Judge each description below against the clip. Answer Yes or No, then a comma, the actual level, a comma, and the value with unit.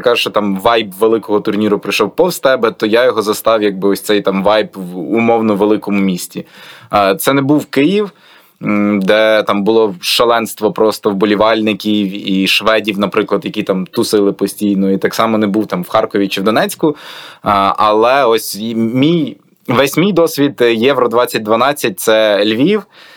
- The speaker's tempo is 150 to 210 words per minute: Yes, fast, 155 wpm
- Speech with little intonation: Yes, narrow, 2.0 semitones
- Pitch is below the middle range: Yes, low, 105 Hz